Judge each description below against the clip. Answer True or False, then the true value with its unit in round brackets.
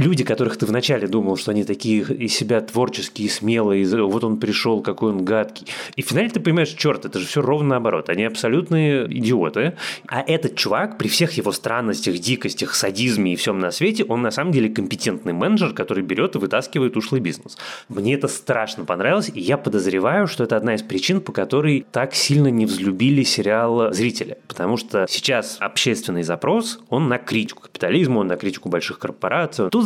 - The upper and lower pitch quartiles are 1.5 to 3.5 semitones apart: False (5.0 semitones)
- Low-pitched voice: True (115 Hz)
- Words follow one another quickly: True (185 wpm)